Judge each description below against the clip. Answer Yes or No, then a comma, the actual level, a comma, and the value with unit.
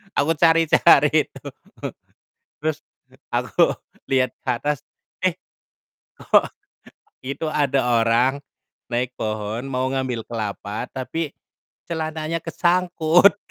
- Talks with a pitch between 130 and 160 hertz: Yes, medium, 140 Hz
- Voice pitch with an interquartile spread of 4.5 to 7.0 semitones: Yes, average, 4.8 semitones